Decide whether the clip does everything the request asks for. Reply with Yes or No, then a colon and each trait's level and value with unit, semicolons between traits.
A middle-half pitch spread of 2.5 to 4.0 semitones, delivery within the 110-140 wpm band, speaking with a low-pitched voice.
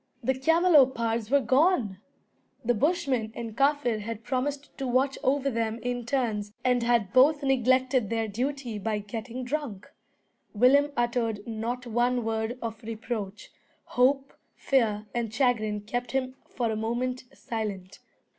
No: average, 3.0 semitones; slow, 135 wpm; high, 240 Hz